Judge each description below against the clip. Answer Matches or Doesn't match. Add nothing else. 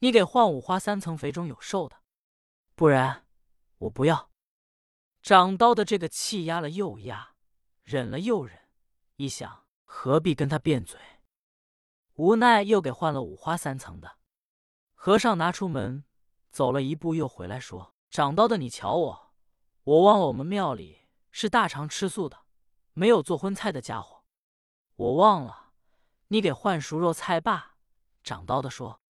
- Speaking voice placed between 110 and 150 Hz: Doesn't match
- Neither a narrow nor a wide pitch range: Doesn't match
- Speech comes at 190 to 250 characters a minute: Matches